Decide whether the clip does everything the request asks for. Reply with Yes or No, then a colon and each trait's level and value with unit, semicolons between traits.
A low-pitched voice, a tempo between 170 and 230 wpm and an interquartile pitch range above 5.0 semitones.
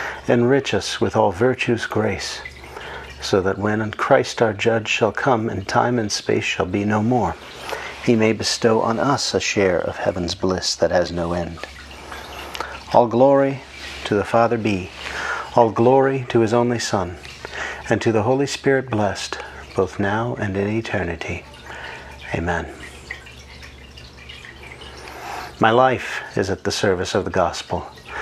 No: low, 110 Hz; average, 145 wpm; wide, 5.4 semitones